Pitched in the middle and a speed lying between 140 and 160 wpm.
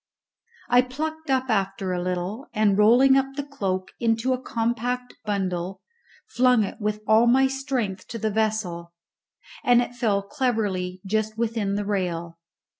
No: high, 220 Hz; average, 150 wpm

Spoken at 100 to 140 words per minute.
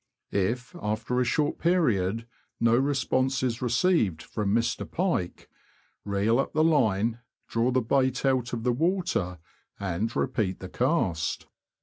Yes: slow, 135 wpm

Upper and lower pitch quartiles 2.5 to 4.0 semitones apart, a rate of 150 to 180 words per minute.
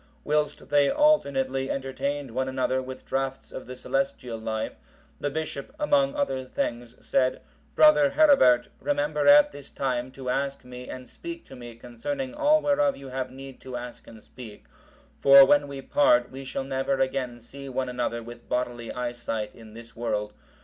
Yes: average, 2.9 semitones; average, 170 wpm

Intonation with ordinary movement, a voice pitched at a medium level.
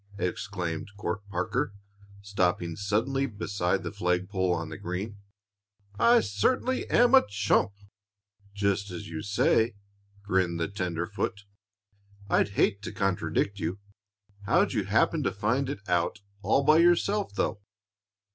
No: average, 3.2 semitones; low, 100 Hz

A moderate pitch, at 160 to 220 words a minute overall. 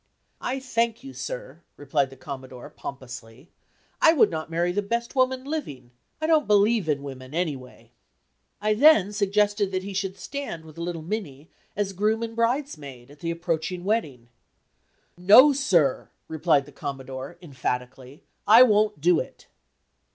No: medium, 180 Hz; average, 150 wpm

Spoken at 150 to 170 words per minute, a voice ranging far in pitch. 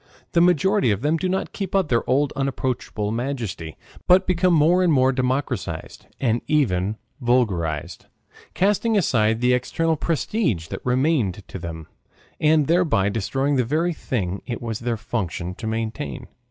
Yes: average, 155 wpm; wide, 6.8 semitones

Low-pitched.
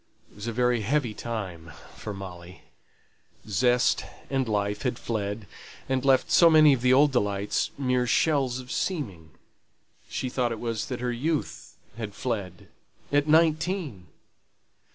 Yes: low, 120 Hz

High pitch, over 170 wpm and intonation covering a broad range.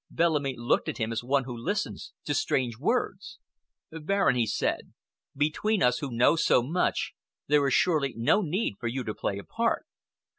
No: medium, 140 Hz; average, 180 wpm; wide, 6.8 semitones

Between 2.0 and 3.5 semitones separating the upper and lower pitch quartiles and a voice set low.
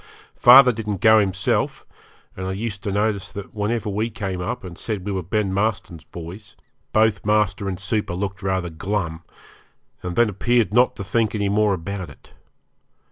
Yes: narrow, 2.5 semitones; low, 100 Hz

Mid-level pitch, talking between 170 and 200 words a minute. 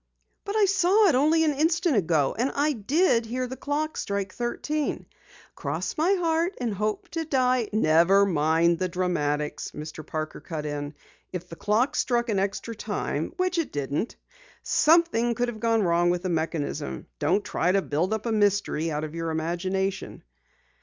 No: high, 210 Hz; average, 175 wpm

